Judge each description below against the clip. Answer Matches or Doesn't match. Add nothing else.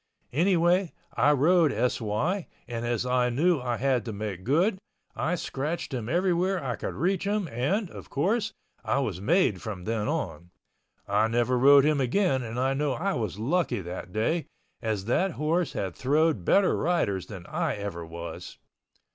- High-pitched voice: Doesn't match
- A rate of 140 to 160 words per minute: Doesn't match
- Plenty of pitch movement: Matches